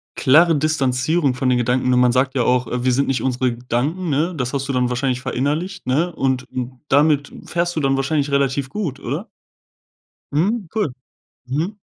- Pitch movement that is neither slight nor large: Yes, average, 3.7 semitones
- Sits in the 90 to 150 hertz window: Yes, low, 135 Hz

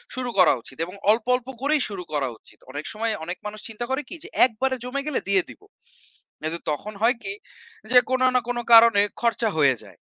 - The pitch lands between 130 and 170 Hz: No, high, 230 Hz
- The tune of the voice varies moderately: No, wide, 5.7 semitones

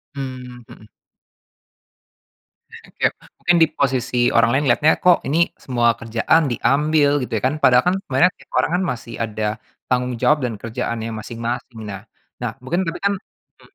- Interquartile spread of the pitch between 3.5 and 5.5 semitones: Yes, average, 4.3 semitones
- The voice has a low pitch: Yes, low, 125 Hz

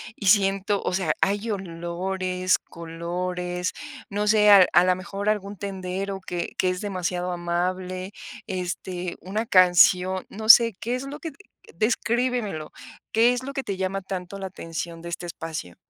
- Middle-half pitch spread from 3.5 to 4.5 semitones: No, narrow, 2.4 semitones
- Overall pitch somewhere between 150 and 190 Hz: Yes, medium, 185 Hz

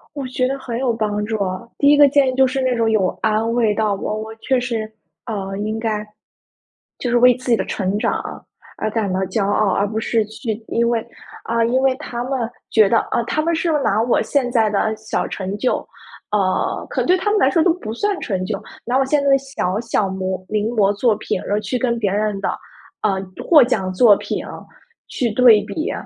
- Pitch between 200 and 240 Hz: Yes, high, 225 Hz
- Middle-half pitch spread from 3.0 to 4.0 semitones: Yes, average, 3.6 semitones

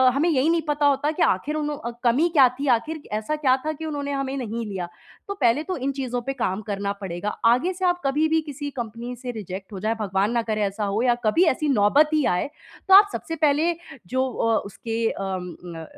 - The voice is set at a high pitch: Yes, very high, 255 Hz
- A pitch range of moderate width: No, wide, 5.9 semitones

